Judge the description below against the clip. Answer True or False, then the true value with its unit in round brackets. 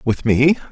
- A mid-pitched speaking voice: False (130 Hz)